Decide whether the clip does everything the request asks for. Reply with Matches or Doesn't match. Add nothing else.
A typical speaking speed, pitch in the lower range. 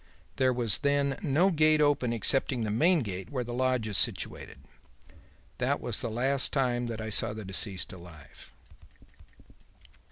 Matches